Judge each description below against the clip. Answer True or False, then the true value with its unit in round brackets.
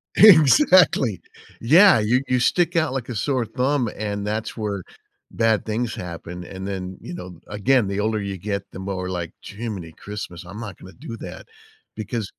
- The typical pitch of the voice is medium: False (105 Hz)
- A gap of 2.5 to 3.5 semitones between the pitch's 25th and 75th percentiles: False (4.7 semitones)